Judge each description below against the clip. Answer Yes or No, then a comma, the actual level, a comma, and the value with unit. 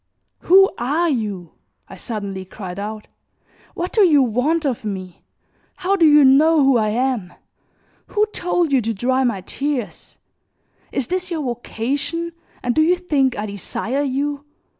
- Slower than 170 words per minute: Yes, average, 155 wpm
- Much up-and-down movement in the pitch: Yes, wide, 6.5 semitones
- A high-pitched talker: Yes, very high, 265 Hz